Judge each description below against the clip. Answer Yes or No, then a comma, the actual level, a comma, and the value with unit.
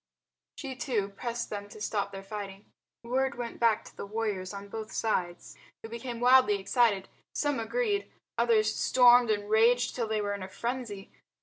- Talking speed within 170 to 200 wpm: Yes, average, 175 wpm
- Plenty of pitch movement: No, average, 3.2 semitones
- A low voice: No, high, 225 Hz